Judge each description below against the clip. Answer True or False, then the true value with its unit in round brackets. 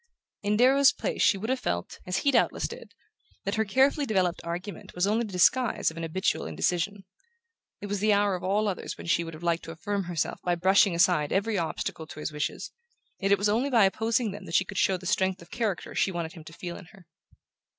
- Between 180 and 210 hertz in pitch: True (190 Hz)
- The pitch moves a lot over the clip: False (3.7 semitones)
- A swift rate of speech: True (235 wpm)